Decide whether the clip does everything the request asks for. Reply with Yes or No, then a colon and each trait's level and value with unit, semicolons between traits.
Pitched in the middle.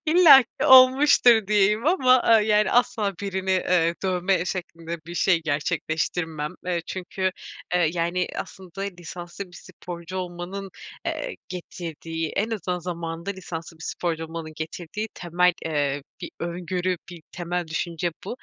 Yes: medium, 180 Hz